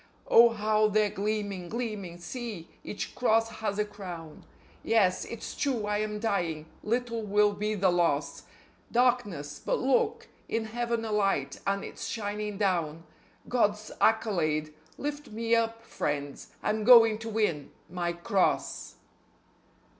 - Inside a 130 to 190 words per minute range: Yes, slow, 135 wpm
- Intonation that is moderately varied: Yes, average, 3.7 semitones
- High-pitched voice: Yes, high, 210 Hz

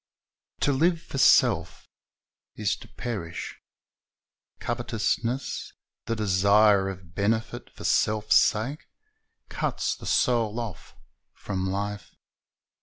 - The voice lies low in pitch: Yes, low, 105 Hz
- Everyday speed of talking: No, slow, 100 wpm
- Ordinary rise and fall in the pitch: Yes, average, 3.2 semitones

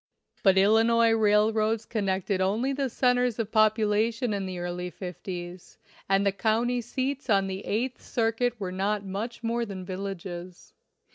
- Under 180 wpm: Yes, average, 150 wpm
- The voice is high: Yes, high, 210 Hz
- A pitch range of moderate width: Yes, average, 3.3 semitones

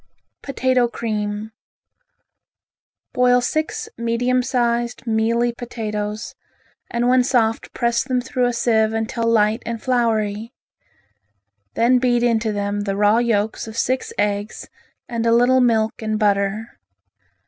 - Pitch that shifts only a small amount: Yes, narrow, 2.1 semitones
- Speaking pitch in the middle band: No, high, 230 Hz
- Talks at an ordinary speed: No, slow, 125 wpm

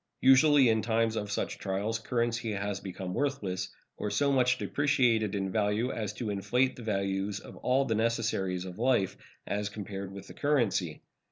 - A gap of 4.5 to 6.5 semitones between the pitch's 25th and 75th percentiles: No, average, 3.8 semitones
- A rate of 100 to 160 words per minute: No, average, 170 wpm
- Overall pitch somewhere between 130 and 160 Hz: No, low, 110 Hz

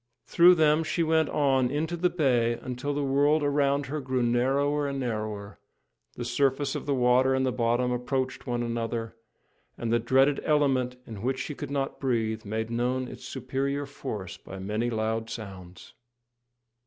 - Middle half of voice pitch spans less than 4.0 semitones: Yes, average, 3.4 semitones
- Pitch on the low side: Yes, low, 130 Hz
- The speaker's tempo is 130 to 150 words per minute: No, average, 165 wpm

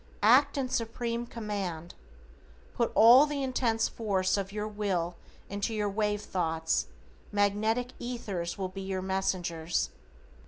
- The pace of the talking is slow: Yes, slow, 125 wpm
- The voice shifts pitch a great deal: No, average, 3.7 semitones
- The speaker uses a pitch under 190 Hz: No, high, 205 Hz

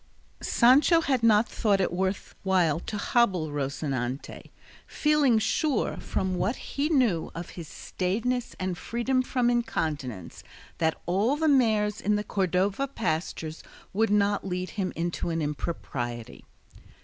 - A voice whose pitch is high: Yes, high, 195 Hz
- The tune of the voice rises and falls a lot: Yes, wide, 6.2 semitones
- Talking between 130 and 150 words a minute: Yes, slow, 135 wpm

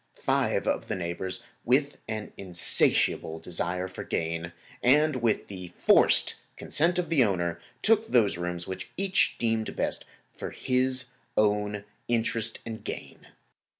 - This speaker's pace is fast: No, slow, 135 wpm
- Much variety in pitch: Yes, wide, 6.1 semitones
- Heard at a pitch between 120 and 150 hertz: No, low, 105 Hz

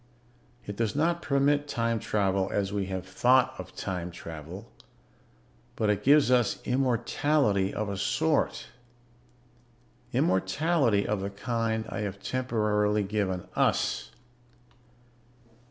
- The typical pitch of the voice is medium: No, low, 105 Hz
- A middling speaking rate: No, slow, 115 wpm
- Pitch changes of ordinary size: Yes, average, 4.6 semitones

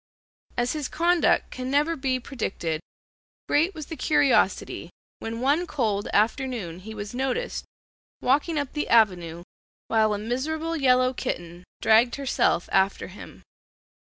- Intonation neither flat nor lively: No, wide, 5.7 semitones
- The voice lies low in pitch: No, very high, 255 Hz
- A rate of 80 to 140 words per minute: Yes, slow, 135 wpm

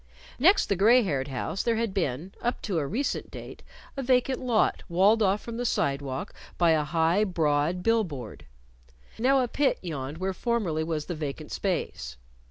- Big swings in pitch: Yes, wide, 7.1 semitones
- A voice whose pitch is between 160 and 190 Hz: Yes, medium, 185 Hz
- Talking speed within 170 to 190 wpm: Yes, average, 175 wpm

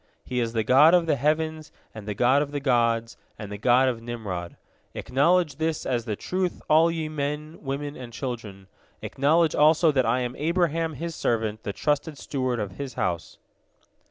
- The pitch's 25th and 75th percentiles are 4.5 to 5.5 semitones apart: Yes, average, 5.1 semitones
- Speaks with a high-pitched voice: No, low, 135 Hz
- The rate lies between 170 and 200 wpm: Yes, average, 185 wpm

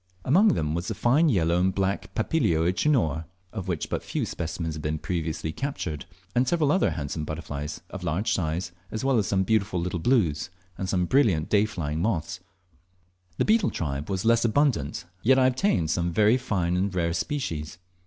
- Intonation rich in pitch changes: Yes, wide, 6.5 semitones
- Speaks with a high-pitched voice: No, very low, 90 Hz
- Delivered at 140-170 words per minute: No, average, 180 wpm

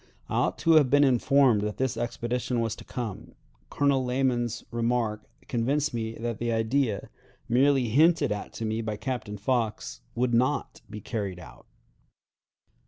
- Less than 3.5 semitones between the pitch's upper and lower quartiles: Yes, average, 3.0 semitones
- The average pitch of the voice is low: Yes, low, 120 Hz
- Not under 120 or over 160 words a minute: Yes, average, 155 wpm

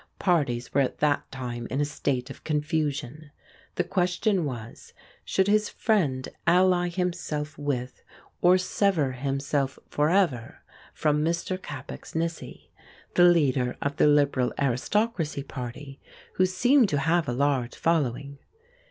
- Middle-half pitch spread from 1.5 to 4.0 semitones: No, average, 4.7 semitones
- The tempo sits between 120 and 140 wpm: Yes, slow, 135 wpm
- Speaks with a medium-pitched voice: Yes, medium, 150 Hz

